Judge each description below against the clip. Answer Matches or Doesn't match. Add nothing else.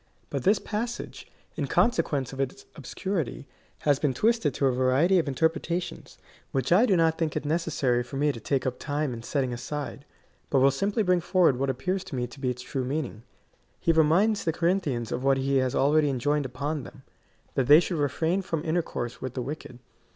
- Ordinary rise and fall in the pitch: Matches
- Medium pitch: Matches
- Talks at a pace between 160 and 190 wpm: Doesn't match